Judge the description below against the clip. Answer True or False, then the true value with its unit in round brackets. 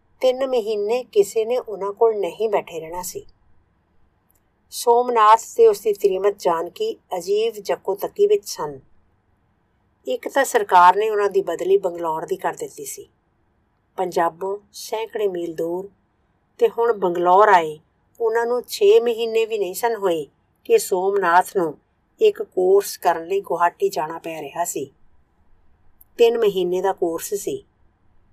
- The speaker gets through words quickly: False (140 wpm)